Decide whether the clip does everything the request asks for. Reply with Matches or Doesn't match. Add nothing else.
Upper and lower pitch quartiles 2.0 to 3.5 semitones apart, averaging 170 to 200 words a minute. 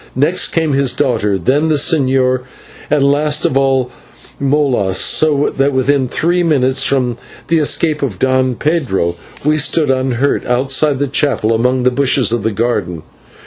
Doesn't match